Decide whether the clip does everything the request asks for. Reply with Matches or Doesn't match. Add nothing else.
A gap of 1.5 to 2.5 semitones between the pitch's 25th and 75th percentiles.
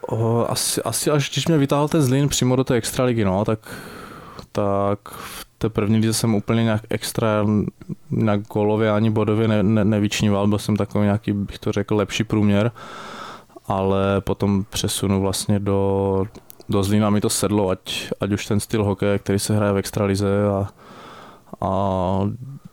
Matches